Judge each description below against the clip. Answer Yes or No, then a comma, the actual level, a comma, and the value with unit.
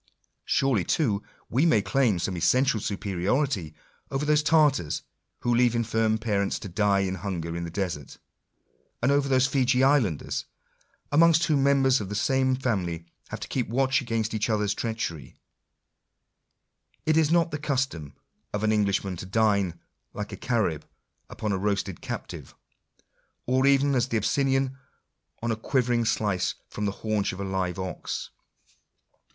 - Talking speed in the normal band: Yes, average, 155 wpm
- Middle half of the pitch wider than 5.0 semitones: Yes, wide, 5.4 semitones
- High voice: No, low, 110 Hz